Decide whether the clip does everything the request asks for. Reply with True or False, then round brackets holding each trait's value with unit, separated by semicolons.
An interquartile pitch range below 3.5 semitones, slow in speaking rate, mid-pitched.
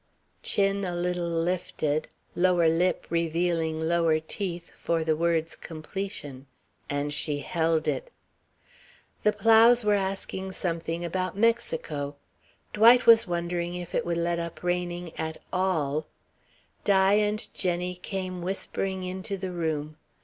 True (2.7 semitones; 125 wpm; 175 Hz)